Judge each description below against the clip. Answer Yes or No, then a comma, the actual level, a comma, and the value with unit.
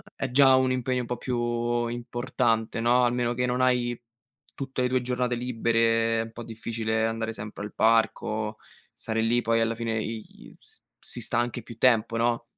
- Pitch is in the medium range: No, low, 120 Hz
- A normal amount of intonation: No, narrow, 1.5 semitones